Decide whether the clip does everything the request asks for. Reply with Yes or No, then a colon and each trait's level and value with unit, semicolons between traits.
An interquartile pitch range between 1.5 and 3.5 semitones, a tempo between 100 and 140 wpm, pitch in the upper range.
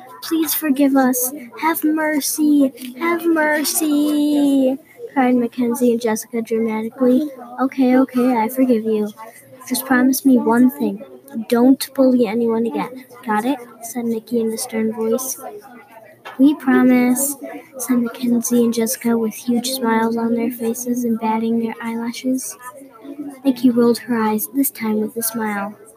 Yes: average, 2.8 semitones; slow, 135 wpm; very high, 250 Hz